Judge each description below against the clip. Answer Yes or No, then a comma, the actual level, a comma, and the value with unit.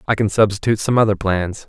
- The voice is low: Yes, low, 105 Hz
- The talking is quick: Yes, fast, 215 wpm